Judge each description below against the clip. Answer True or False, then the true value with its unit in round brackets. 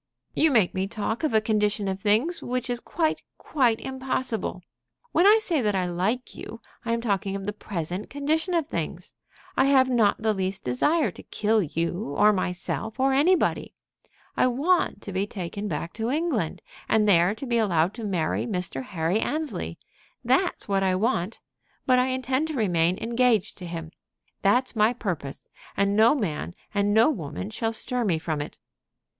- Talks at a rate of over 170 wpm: True (180 wpm)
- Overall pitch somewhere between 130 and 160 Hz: False (215 Hz)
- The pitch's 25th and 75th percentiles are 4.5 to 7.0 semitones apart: True (5.2 semitones)